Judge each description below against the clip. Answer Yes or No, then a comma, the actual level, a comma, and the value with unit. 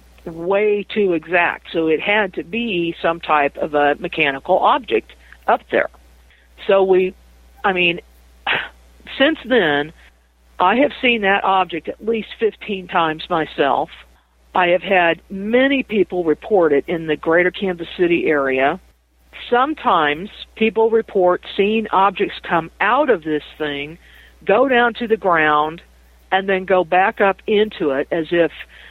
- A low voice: No, medium, 180 Hz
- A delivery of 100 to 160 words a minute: Yes, average, 145 wpm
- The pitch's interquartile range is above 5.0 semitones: Yes, wide, 5.6 semitones